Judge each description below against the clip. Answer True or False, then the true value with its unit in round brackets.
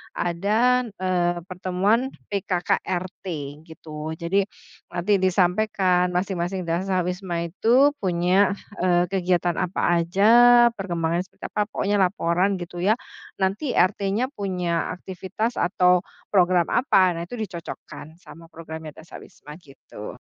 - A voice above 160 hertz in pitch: True (185 Hz)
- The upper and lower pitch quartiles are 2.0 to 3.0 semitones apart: True (2.5 semitones)